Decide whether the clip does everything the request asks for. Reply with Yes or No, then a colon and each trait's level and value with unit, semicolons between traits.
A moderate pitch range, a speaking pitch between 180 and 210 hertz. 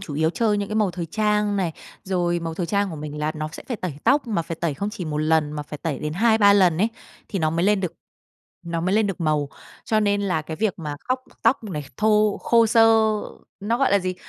Yes: average, 4.8 semitones; medium, 185 Hz